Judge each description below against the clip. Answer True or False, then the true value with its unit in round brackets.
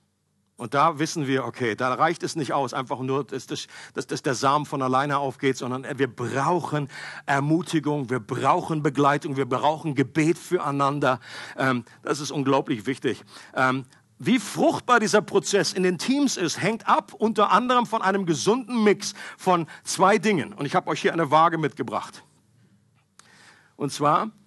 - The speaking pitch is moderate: True (150 Hz)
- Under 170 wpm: True (150 wpm)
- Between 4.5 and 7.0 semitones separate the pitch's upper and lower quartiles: True (5.1 semitones)